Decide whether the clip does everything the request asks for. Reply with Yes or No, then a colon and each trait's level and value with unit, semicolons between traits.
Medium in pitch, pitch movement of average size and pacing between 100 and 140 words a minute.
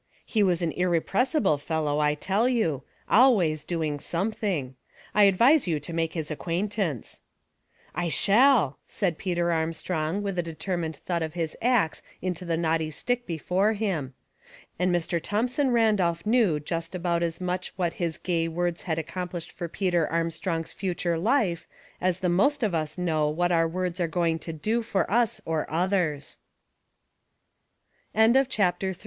Yes: medium, 175 Hz; average, 3.3 semitones; slow, 135 wpm